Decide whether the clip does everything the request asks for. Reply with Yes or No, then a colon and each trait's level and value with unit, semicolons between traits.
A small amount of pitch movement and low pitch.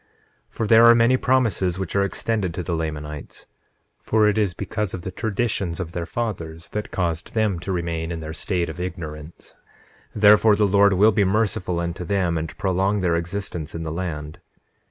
No: average, 3.9 semitones; very low, 90 Hz